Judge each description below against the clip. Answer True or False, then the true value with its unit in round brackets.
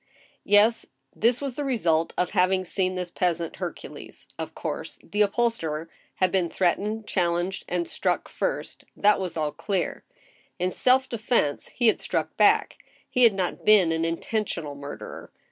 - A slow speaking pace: False (160 wpm)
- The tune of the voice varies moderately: True (4.4 semitones)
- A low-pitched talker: False (185 Hz)